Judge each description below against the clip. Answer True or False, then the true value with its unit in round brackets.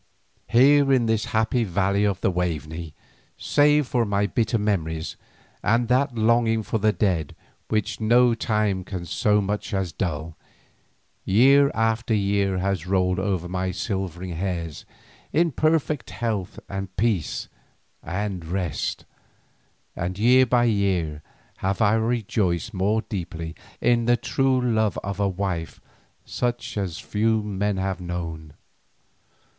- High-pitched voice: False (100 Hz)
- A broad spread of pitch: False (4.0 semitones)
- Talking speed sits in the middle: False (130 wpm)